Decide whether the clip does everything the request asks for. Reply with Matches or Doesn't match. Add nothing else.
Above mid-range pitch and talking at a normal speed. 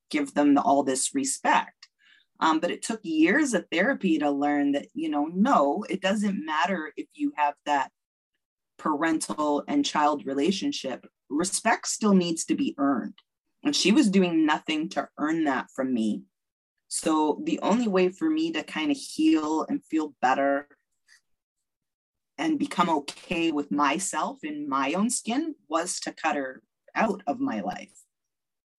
Matches